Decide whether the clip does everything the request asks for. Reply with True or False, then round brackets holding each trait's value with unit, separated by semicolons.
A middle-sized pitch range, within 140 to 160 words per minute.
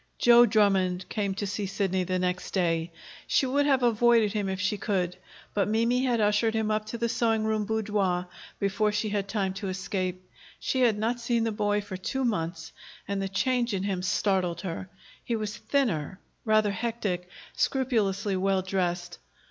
False (3.1 semitones; 180 wpm)